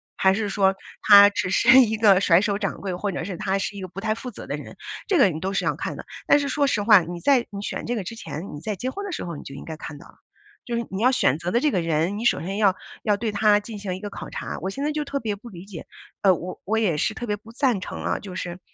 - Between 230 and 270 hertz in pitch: No, high, 205 Hz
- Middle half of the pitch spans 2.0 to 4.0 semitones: Yes, average, 3.7 semitones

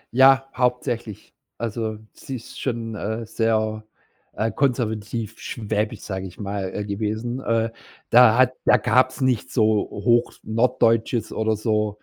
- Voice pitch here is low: Yes, low, 115 Hz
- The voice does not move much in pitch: Yes, narrow, 2.3 semitones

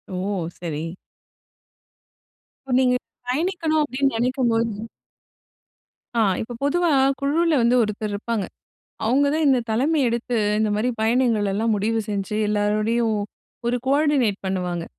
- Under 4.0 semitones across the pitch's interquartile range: No, average, 4.5 semitones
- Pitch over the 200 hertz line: Yes, high, 235 Hz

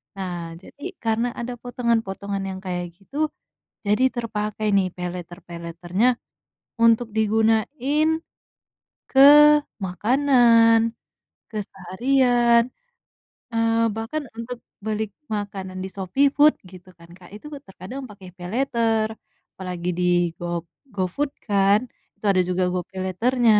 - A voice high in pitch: Yes, high, 215 Hz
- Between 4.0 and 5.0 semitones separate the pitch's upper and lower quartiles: Yes, average, 4.3 semitones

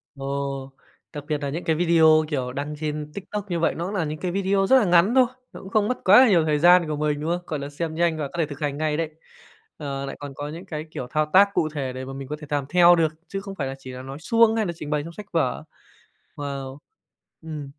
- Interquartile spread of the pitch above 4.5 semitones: No, average, 3.7 semitones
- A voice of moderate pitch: Yes, medium, 155 Hz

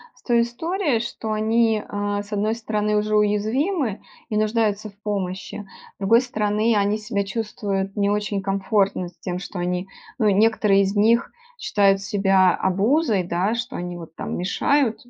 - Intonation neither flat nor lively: No, narrow, 2.3 semitones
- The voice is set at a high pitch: Yes, high, 210 Hz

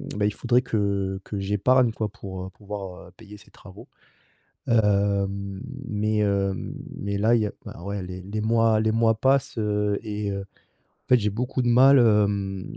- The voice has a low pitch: Yes, low, 105 Hz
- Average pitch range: No, narrow, 2.3 semitones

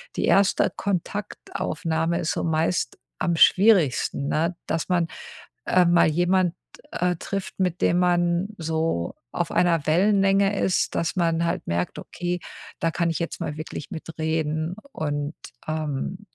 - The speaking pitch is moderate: Yes, medium, 170 Hz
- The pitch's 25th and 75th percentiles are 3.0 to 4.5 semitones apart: No, narrow, 2.4 semitones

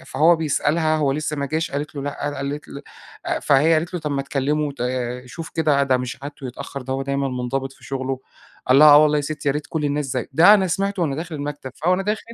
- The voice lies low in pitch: No, medium, 145 Hz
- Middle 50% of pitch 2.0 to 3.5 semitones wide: Yes, narrow, 2.5 semitones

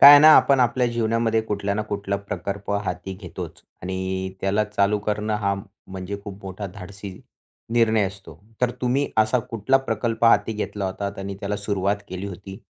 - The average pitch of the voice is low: Yes, low, 105 Hz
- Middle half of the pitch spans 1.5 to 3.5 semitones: Yes, narrow, 2.4 semitones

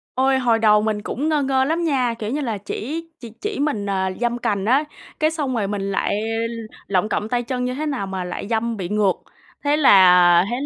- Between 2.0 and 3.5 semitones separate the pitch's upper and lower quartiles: No, average, 5.1 semitones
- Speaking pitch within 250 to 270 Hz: No, high, 235 Hz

